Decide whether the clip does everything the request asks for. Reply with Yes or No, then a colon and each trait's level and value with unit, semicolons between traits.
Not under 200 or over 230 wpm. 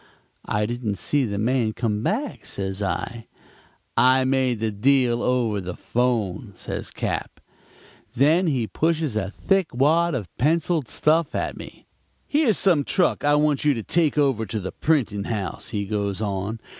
No: average, 160 wpm